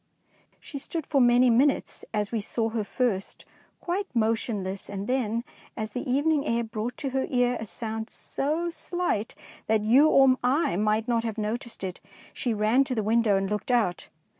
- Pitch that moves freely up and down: No, average, 3.6 semitones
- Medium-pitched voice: No, high, 235 Hz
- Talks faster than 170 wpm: Yes, average, 180 wpm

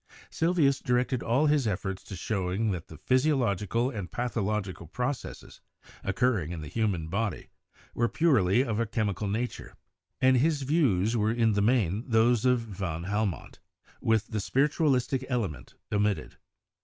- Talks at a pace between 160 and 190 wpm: No, average, 145 wpm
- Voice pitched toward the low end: Yes, low, 110 Hz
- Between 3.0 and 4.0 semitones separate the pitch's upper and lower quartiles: No, average, 4.4 semitones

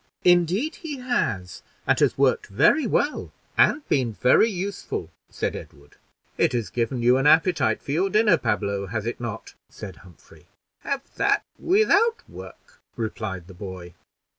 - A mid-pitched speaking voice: No, low, 130 Hz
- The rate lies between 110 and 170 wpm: Yes, average, 150 wpm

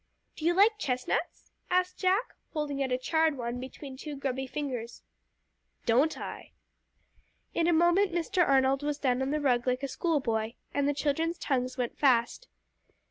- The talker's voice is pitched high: Yes, very high, 280 Hz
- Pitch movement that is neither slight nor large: Yes, average, 4.4 semitones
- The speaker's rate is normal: Yes, average, 170 wpm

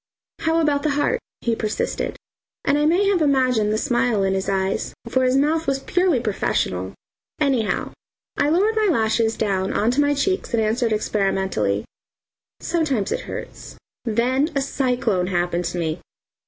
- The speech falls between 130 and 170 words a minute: Yes, average, 160 wpm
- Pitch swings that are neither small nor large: No, wide, 6.4 semitones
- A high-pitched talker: Yes, high, 245 Hz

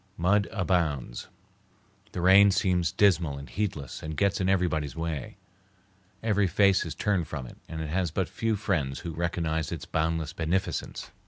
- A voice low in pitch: Yes, very low, 85 Hz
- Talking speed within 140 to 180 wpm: Yes, average, 160 wpm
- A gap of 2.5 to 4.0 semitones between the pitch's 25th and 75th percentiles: Yes, average, 3.5 semitones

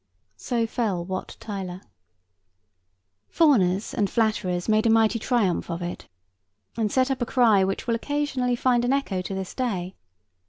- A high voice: Yes, high, 220 Hz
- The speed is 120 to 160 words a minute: Yes, average, 155 wpm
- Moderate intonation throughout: Yes, average, 4.5 semitones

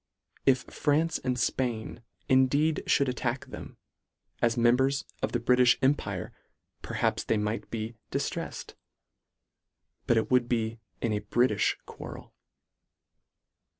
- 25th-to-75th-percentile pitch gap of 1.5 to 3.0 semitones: Yes, narrow, 2.6 semitones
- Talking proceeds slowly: Yes, slow, 120 wpm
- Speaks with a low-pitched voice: Yes, low, 125 Hz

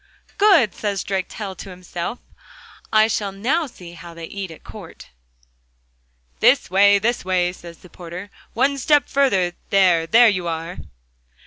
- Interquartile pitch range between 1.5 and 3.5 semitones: No, average, 4.2 semitones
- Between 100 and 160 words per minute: Yes, average, 145 wpm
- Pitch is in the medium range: No, high, 195 Hz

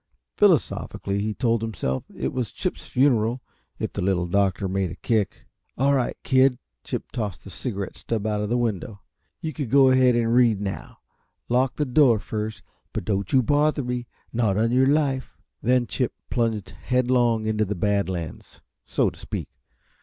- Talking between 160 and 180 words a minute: Yes, average, 175 wpm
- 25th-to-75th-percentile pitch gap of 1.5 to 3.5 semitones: No, average, 4.0 semitones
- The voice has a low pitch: Yes, low, 115 Hz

